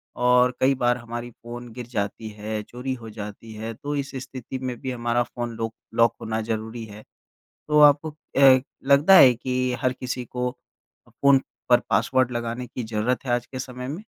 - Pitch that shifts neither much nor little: No, narrow, 2.1 semitones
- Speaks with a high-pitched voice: No, low, 125 Hz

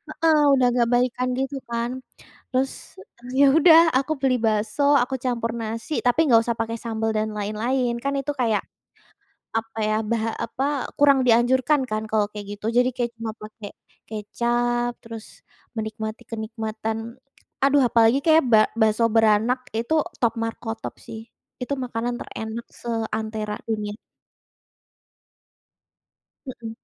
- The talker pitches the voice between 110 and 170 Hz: No, high, 235 Hz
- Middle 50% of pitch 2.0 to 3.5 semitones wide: Yes, average, 2.7 semitones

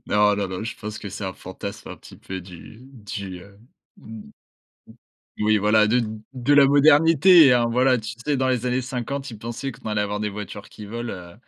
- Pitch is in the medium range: No, low, 110 Hz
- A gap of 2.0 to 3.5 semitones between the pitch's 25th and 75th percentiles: No, average, 4.1 semitones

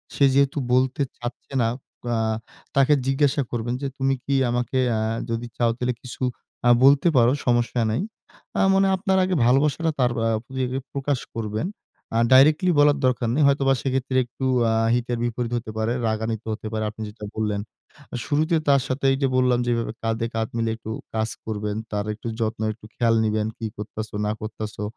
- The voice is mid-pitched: No, low, 120 Hz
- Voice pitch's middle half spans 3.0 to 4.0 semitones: Yes, average, 3.4 semitones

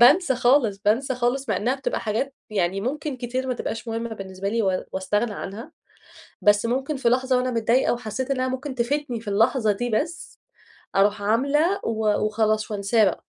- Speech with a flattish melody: No, average, 3.7 semitones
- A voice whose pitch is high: Yes, high, 235 Hz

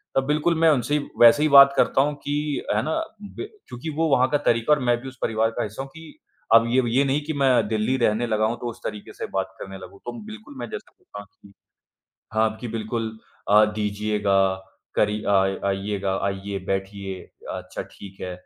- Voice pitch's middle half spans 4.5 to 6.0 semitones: Yes, average, 5.2 semitones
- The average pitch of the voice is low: Yes, low, 115 Hz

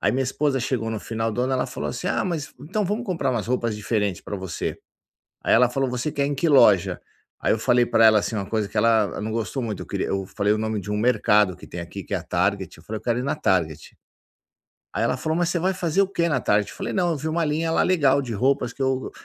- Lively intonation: Yes, wide, 5.7 semitones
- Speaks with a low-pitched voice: Yes, low, 120 Hz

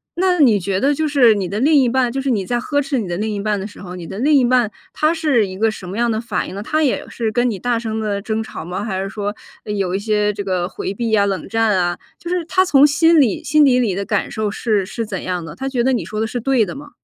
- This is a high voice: Yes, high, 220 Hz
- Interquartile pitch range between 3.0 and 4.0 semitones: No, average, 4.9 semitones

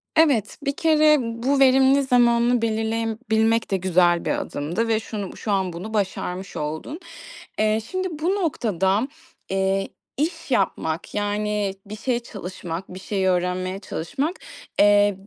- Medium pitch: No, high, 215 Hz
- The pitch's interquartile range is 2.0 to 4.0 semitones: No, average, 4.9 semitones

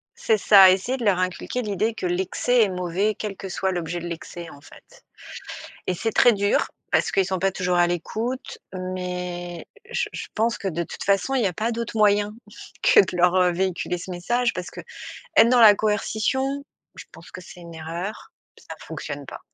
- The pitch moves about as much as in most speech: Yes, average, 3.4 semitones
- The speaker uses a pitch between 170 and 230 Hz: Yes, high, 190 Hz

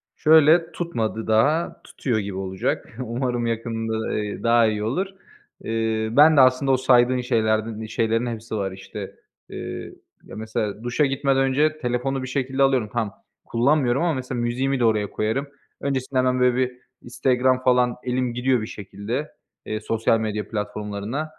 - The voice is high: No, low, 120 Hz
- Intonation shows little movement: No, average, 3.1 semitones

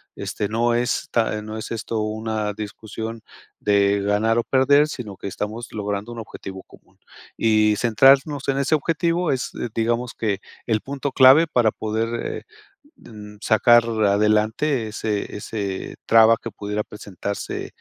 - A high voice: No, low, 110 Hz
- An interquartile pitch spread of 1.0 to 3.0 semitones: Yes, narrow, 2.5 semitones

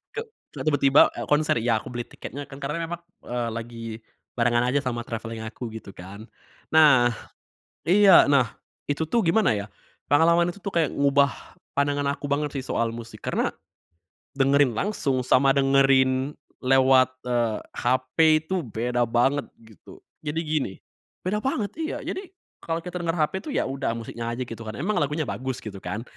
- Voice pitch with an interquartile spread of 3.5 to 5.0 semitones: Yes, average, 4.3 semitones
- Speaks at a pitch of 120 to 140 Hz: Yes, low, 135 Hz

